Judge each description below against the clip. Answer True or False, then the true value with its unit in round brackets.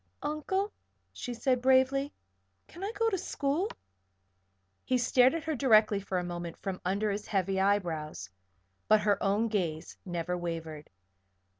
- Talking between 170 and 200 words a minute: False (145 wpm)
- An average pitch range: False (7.4 semitones)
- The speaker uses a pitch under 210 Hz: False (215 Hz)